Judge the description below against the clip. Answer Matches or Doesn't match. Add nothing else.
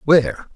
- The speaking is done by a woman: Doesn't match